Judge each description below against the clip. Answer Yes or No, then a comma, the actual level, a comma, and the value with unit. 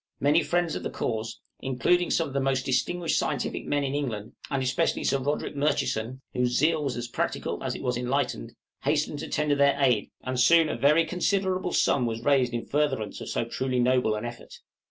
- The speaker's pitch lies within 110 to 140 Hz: Yes, low, 135 Hz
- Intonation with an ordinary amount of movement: Yes, average, 3.4 semitones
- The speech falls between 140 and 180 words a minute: No, average, 200 wpm